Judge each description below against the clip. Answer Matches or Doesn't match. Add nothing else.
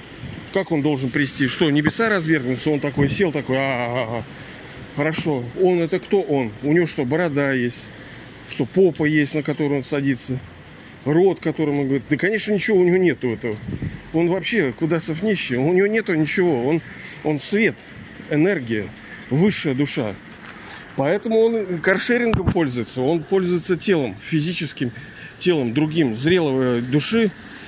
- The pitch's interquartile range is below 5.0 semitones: Doesn't match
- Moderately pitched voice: Matches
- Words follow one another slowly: Doesn't match